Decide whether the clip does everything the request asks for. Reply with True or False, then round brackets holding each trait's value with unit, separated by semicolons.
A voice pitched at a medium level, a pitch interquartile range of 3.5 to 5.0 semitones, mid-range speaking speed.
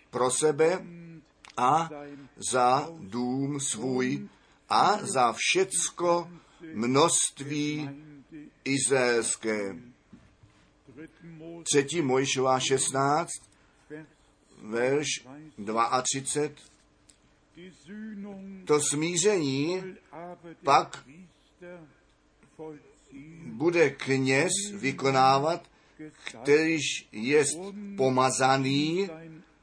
False (150 Hz; 3.8 semitones; 50 wpm)